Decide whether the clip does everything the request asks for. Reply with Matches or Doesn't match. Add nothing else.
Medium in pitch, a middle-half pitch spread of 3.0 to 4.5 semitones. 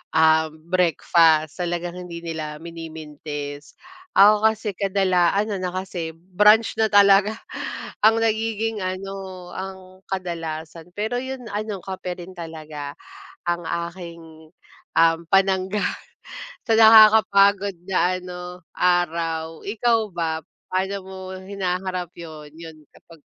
Matches